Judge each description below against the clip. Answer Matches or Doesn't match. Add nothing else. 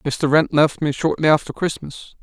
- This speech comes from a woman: Doesn't match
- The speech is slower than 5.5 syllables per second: Matches